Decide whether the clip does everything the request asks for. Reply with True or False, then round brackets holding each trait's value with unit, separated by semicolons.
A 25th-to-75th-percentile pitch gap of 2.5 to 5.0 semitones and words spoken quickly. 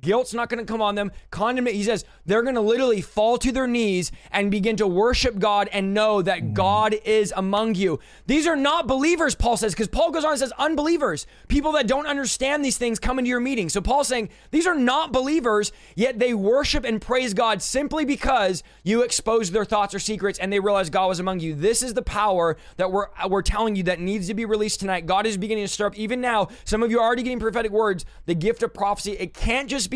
True (3.8 semitones; 240 wpm)